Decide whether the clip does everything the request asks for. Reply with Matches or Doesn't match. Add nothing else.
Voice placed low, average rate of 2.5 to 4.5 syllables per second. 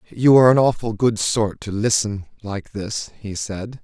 Matches